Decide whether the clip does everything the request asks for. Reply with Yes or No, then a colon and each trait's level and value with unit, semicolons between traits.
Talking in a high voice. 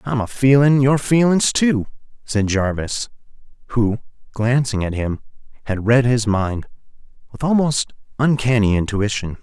No: low, 120 Hz